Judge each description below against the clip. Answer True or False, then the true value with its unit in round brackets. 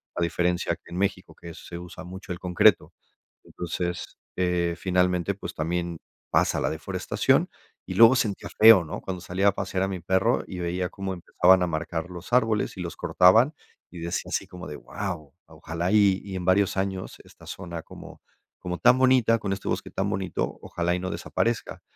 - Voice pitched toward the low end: True (90 Hz)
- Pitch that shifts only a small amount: True (2.0 semitones)